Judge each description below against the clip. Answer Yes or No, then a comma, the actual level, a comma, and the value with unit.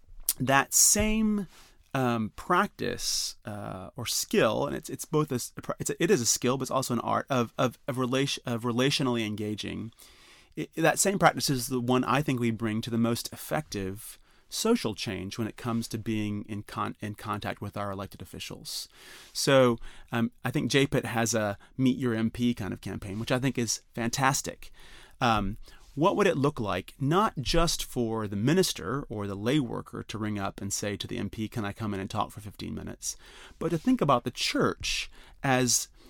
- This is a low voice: Yes, low, 120 Hz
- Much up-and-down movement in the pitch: No, average, 4.0 semitones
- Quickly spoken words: No, average, 195 wpm